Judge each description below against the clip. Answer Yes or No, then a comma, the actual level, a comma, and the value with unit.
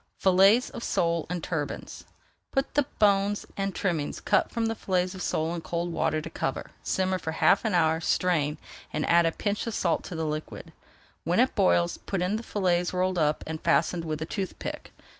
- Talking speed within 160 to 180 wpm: No, average, 195 wpm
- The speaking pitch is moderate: Yes, medium, 175 Hz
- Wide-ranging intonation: No, average, 3.3 semitones